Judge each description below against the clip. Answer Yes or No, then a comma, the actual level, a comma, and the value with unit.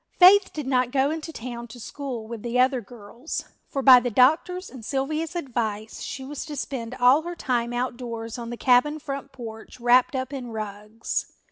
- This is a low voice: No, very high, 250 Hz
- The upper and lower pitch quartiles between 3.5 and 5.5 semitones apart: No, average, 3.0 semitones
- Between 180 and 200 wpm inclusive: Yes, average, 190 wpm